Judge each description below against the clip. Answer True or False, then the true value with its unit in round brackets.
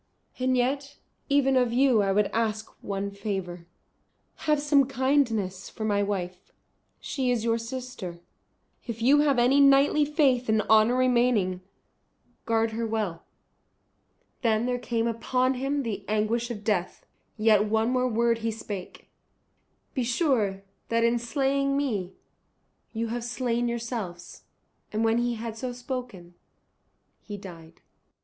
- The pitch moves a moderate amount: True (3.4 semitones)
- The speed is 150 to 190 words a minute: False (140 wpm)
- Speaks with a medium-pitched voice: False (230 Hz)